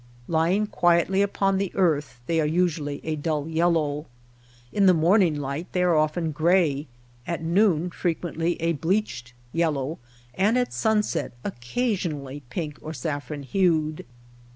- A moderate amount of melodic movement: Yes, average, 3.4 semitones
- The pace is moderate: Yes, average, 145 wpm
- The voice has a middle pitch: Yes, medium, 165 Hz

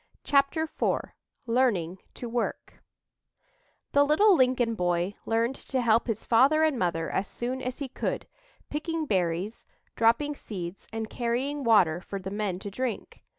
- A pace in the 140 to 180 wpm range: Yes, average, 150 wpm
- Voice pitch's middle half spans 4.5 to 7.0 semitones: Yes, wide, 5.6 semitones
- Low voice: No, high, 235 Hz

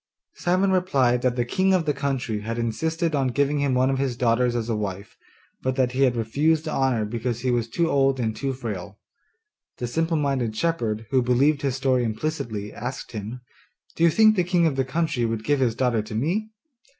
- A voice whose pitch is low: Yes, low, 130 Hz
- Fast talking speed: Yes, fast, 210 wpm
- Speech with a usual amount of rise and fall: Yes, average, 4.3 semitones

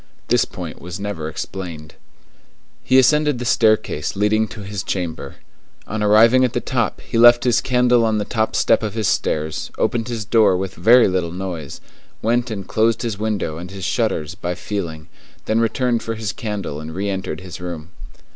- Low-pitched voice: Yes, low, 105 Hz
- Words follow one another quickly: No, average, 185 wpm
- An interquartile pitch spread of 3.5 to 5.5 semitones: Yes, average, 4.4 semitones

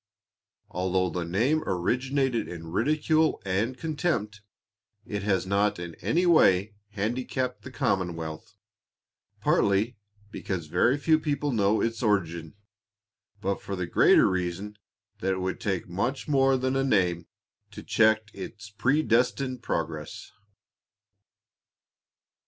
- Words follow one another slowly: Yes, slow, 120 wpm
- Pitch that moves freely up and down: Yes, wide, 5.8 semitones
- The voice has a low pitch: Yes, low, 105 Hz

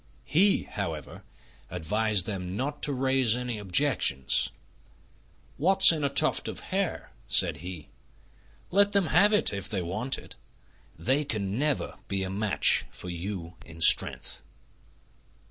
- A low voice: Yes, low, 110 Hz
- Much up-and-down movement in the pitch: Yes, wide, 8.0 semitones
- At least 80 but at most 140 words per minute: Yes, slow, 135 wpm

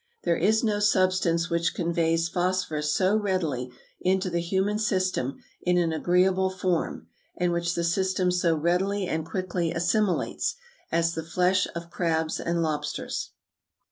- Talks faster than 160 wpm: No, average, 140 wpm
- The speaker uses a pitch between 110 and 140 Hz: No, medium, 175 Hz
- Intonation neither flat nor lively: No, narrow, 2.0 semitones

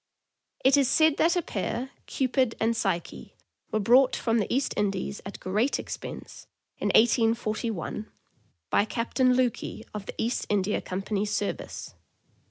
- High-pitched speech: Yes, high, 225 Hz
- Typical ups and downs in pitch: Yes, average, 3.8 semitones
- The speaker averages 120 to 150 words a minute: Yes, average, 145 wpm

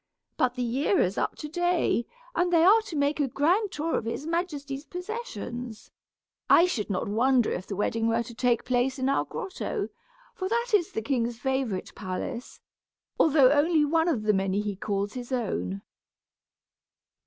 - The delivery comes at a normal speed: Yes, average, 175 wpm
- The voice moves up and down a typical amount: No, wide, 6.4 semitones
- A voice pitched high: Yes, very high, 265 Hz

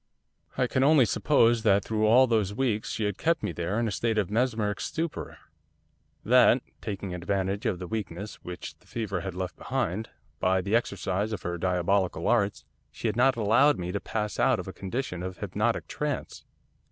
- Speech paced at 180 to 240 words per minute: Yes, average, 190 wpm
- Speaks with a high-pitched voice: No, low, 105 Hz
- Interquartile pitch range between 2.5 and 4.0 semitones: Yes, average, 3.7 semitones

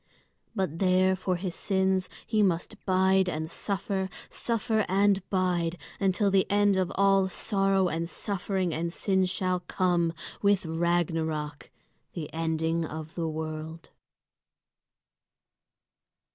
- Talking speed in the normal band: No, slow, 115 wpm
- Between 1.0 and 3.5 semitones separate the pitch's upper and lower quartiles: Yes, average, 2.8 semitones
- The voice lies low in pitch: No, medium, 185 Hz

